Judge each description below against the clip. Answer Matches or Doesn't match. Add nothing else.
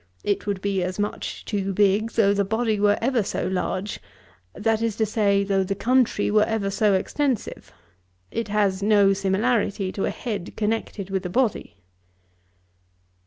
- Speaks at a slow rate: Doesn't match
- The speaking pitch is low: Doesn't match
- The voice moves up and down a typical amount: Doesn't match